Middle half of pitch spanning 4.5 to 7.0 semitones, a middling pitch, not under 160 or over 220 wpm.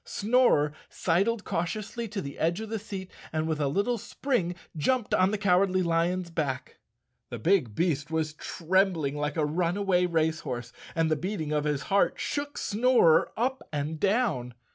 Yes: average, 4.8 semitones; medium, 175 Hz; average, 165 wpm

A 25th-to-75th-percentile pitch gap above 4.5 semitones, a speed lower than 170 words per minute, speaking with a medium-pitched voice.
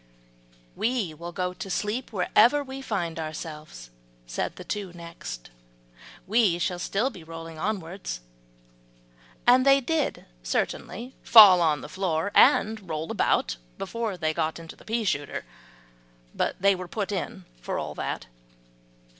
Yes: average, 5.2 semitones; average, 140 wpm; medium, 180 Hz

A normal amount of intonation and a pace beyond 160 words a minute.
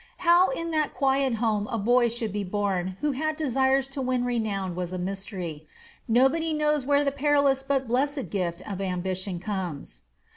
No: wide, 6.5 semitones; average, 175 wpm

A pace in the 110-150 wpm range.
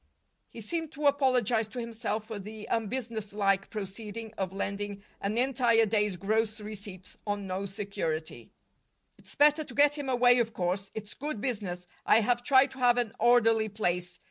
No: average, 165 wpm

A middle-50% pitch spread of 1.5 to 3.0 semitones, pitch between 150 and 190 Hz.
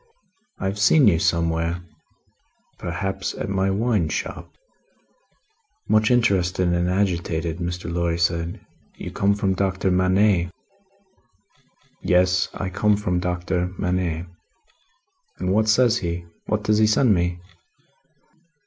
No: average, 2.7 semitones; very low, 90 Hz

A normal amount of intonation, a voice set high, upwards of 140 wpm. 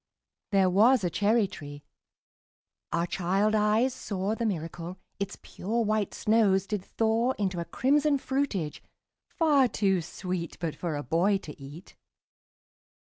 No: average, 4.2 semitones; high, 200 Hz; slow, 135 wpm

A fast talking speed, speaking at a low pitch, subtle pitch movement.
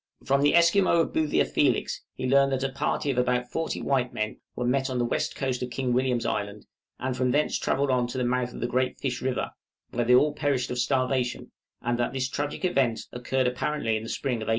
Yes: fast, 235 wpm; low, 130 Hz; narrow, 2.0 semitones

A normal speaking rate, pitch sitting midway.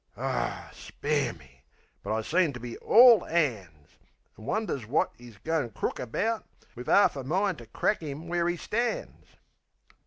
Yes: average, 160 wpm; medium, 145 Hz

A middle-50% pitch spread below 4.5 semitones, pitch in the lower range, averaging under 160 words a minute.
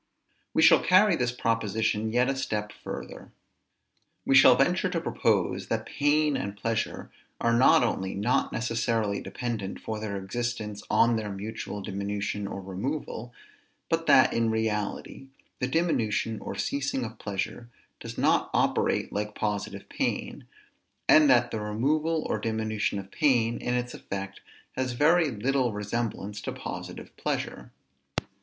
Yes: average, 3.5 semitones; low, 115 Hz; average, 140 wpm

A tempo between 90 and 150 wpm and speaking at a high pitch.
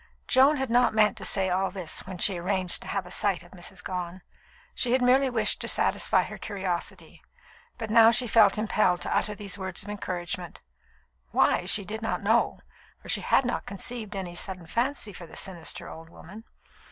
No: average, 195 wpm; high, 195 Hz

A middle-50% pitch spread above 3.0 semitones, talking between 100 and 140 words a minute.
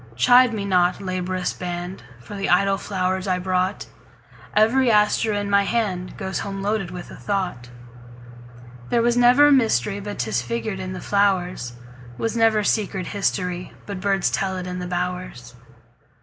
No: average, 2.7 semitones; slow, 135 wpm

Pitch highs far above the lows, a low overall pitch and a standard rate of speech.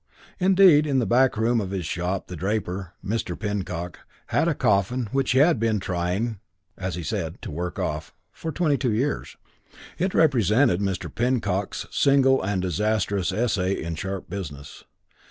Yes: wide, 5.7 semitones; low, 100 Hz; average, 160 wpm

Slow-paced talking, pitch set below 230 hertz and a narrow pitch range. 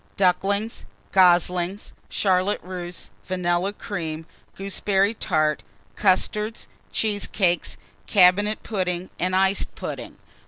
Yes: slow, 85 wpm; medium, 185 Hz; narrow, 2.2 semitones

